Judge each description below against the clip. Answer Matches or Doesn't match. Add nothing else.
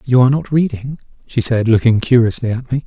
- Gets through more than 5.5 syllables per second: Matches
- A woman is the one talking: Doesn't match